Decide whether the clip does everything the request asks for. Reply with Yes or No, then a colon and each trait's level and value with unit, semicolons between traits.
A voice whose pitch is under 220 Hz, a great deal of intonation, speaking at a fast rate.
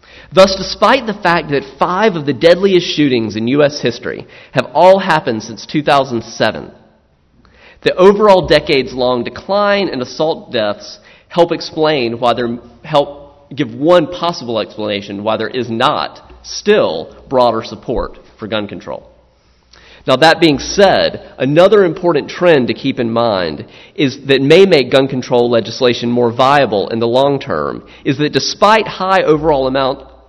No: low, 135 Hz; wide, 6.0 semitones; average, 145 wpm